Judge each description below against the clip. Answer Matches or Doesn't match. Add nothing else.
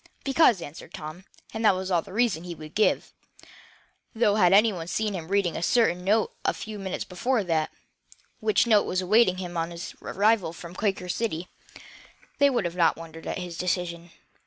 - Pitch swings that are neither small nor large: Matches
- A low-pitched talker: Doesn't match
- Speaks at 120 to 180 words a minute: Doesn't match